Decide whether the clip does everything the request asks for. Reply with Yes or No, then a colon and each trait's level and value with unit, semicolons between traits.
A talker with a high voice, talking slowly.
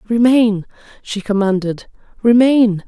Yes: high, 215 Hz; slow, 85 wpm